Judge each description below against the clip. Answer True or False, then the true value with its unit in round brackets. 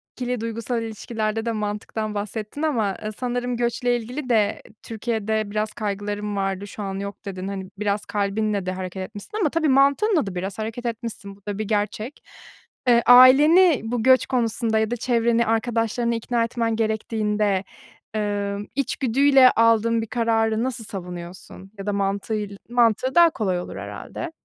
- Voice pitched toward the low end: False (220 Hz)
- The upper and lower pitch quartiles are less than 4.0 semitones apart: True (2.8 semitones)